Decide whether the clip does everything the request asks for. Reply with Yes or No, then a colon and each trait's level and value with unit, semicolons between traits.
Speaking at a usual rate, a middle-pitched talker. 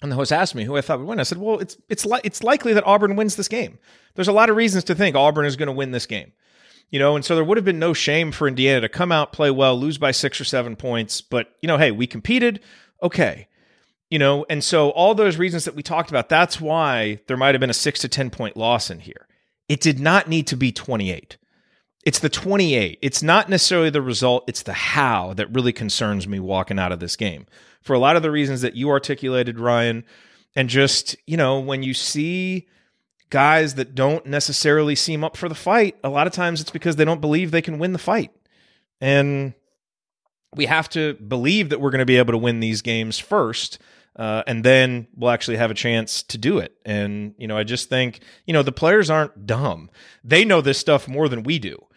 No: fast, 240 wpm; medium, 145 Hz